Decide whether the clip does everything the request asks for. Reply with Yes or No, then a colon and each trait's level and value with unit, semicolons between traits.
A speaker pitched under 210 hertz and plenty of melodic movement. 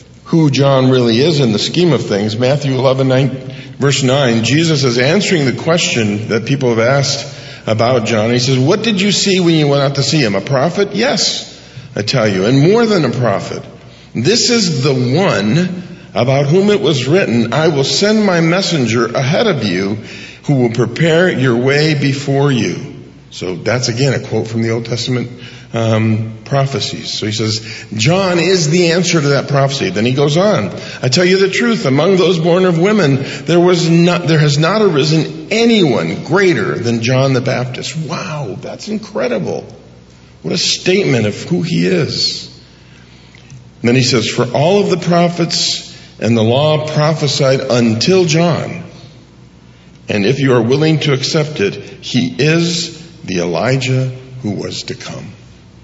Yes: medium, 140 Hz; wide, 5.9 semitones